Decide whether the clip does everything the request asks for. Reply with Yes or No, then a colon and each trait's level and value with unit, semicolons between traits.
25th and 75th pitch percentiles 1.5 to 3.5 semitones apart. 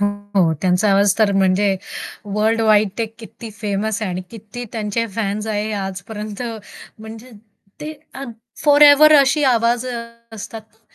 Yes: narrow, 2.5 semitones